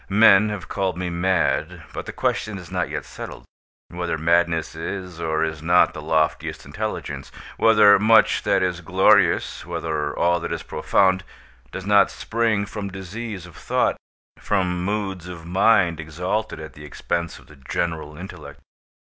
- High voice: No, very low, 90 Hz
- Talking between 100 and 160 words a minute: Yes, average, 145 wpm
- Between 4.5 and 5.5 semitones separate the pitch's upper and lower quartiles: No, average, 3.4 semitones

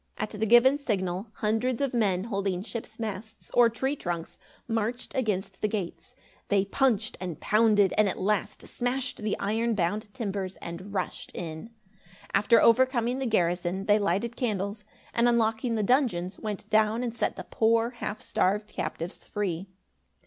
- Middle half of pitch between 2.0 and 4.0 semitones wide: Yes, average, 3.3 semitones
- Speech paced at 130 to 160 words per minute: Yes, average, 155 wpm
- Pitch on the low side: No, high, 215 Hz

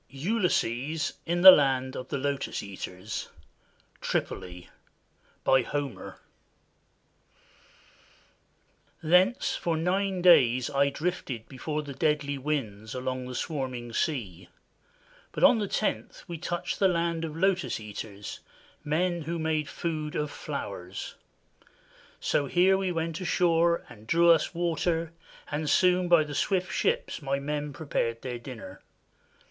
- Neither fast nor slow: No, slow, 125 wpm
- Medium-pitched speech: Yes, medium, 150 Hz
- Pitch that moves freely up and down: No, average, 5.0 semitones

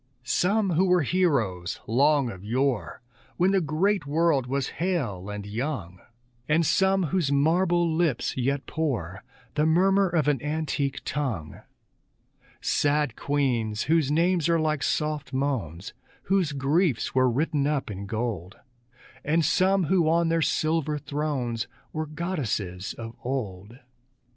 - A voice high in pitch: No, medium, 145 Hz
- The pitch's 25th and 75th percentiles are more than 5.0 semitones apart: Yes, wide, 5.5 semitones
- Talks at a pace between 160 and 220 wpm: No, slow, 135 wpm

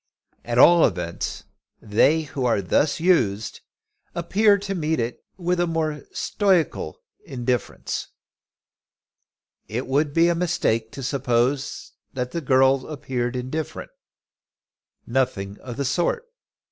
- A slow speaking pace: Yes, slow, 120 wpm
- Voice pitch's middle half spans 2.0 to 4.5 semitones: No, wide, 5.5 semitones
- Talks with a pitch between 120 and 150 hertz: Yes, low, 135 Hz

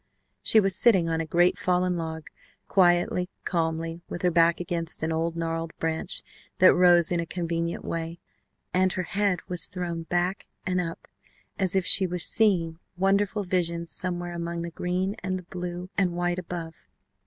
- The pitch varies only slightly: Yes, narrow, 1.6 semitones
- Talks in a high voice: No, medium, 175 Hz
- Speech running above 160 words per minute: Yes, average, 170 wpm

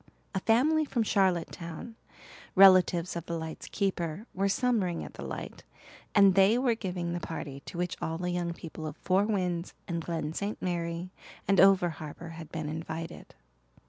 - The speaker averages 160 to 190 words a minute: Yes, average, 170 wpm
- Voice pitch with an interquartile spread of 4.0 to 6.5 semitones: No, average, 2.9 semitones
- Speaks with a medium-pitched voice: Yes, medium, 175 Hz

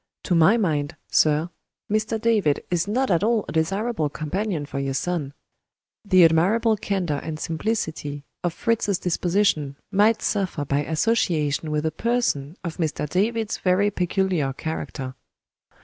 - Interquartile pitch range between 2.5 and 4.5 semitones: No, wide, 5.4 semitones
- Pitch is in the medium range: Yes, medium, 175 Hz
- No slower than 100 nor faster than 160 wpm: Yes, average, 140 wpm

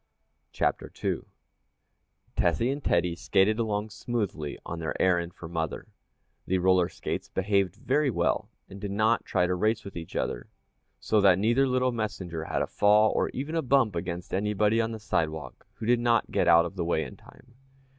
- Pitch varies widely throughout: No, average, 4.7 semitones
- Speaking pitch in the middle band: No, low, 100 Hz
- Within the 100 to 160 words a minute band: No, average, 185 wpm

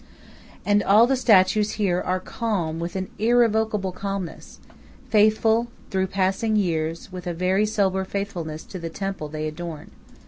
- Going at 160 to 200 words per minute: No, average, 145 wpm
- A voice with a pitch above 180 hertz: Yes, high, 190 Hz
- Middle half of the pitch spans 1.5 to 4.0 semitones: Yes, average, 3.4 semitones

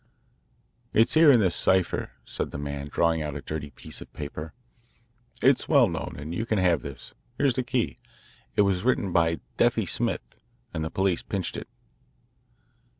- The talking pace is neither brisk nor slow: Yes, average, 170 wpm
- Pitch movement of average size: No, wide, 6.6 semitones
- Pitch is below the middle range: Yes, very low, 85 Hz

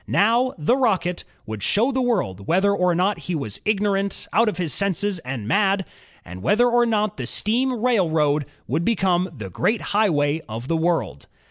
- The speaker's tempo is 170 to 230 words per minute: Yes, average, 175 wpm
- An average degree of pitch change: No, wide, 6.3 semitones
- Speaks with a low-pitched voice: No, high, 190 Hz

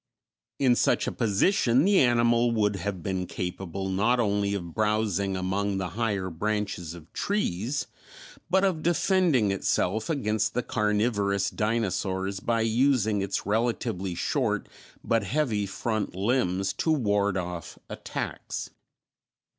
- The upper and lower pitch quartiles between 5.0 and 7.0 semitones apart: No, average, 3.6 semitones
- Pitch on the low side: Yes, low, 105 Hz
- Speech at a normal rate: No, slow, 125 wpm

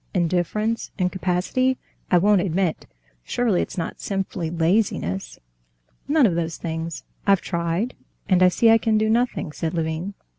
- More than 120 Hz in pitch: Yes, medium, 185 Hz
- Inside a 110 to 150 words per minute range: Yes, average, 140 wpm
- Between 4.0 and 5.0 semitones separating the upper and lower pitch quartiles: Yes, average, 4.4 semitones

